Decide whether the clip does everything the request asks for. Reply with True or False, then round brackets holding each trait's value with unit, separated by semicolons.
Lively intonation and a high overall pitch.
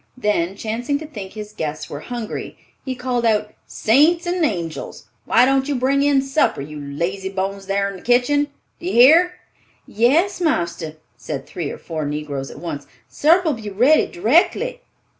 True (8.6 semitones; 220 Hz)